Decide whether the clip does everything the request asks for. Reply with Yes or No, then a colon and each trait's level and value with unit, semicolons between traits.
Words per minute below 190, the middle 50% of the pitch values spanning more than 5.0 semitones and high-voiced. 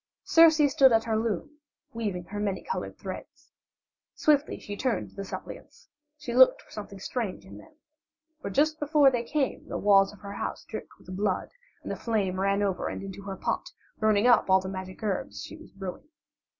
No: average, 195 wpm; wide, 5.6 semitones; high, 210 Hz